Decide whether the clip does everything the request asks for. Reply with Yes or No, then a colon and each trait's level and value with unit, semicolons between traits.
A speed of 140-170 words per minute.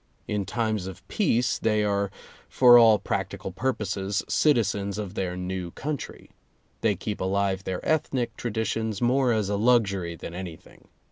Yes: average, 150 wpm